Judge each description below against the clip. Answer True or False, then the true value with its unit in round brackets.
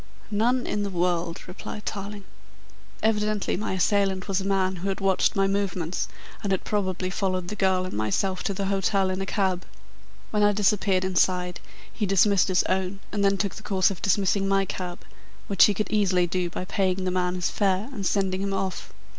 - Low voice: False (195 Hz)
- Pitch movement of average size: False (1.5 semitones)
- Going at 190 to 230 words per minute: True (195 wpm)